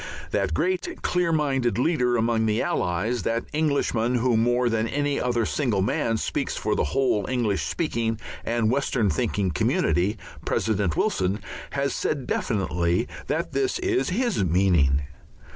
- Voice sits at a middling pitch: No, low, 115 Hz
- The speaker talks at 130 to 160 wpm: Yes, average, 145 wpm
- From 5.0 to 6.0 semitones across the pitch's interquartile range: Yes, wide, 5.4 semitones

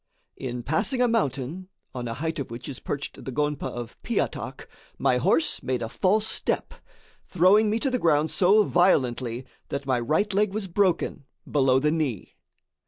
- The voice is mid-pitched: Yes, medium, 150 Hz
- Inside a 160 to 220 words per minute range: Yes, average, 170 wpm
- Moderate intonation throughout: No, wide, 6.8 semitones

